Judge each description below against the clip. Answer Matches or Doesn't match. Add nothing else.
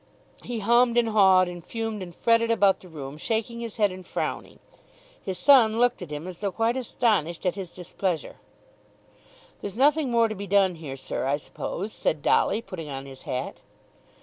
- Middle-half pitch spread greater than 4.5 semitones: Matches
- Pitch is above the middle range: Matches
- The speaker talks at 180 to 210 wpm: Matches